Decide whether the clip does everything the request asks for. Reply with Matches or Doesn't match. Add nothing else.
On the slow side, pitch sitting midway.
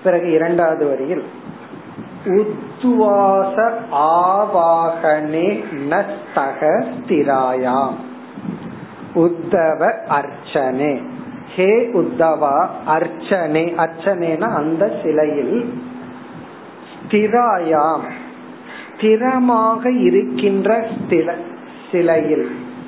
Matches